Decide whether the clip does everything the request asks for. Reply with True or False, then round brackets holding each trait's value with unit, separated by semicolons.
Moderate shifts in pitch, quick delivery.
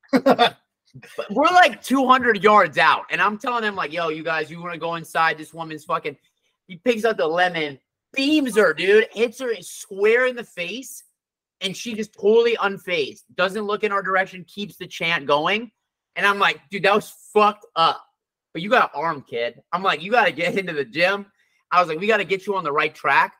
False (6.4 semitones; 220 wpm)